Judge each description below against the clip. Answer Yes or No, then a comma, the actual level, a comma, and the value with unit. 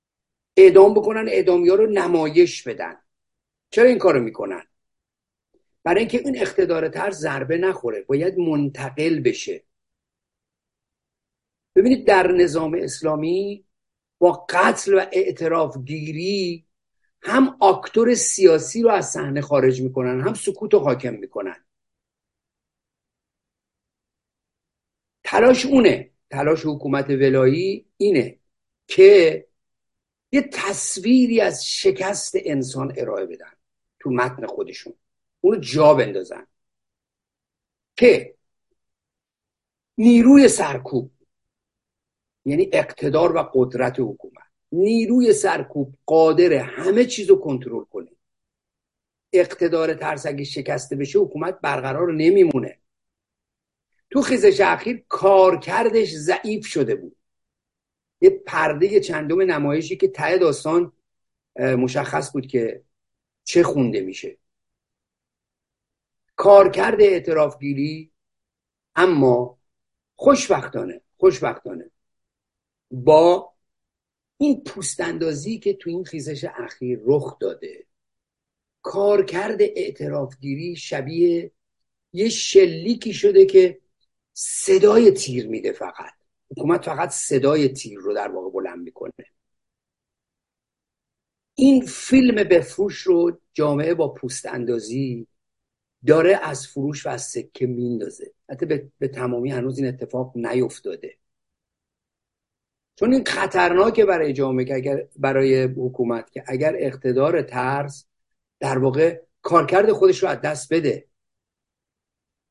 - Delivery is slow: Yes, slow, 100 wpm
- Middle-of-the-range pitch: Yes, medium, 175 Hz